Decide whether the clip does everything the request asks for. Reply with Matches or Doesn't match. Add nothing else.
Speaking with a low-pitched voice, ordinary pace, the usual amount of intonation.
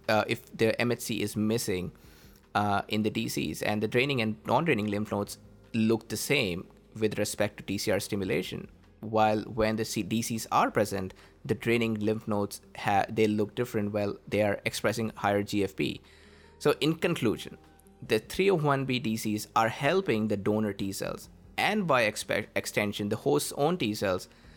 Doesn't match